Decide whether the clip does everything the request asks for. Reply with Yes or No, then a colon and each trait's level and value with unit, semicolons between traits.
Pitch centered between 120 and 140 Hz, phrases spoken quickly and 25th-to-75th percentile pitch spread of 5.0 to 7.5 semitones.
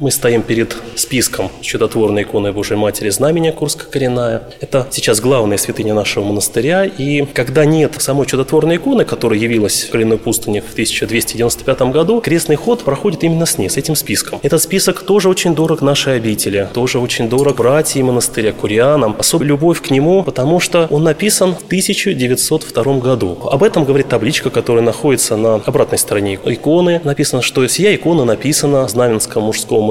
Yes: low, 135 Hz; fast, 165 wpm; wide, 5.6 semitones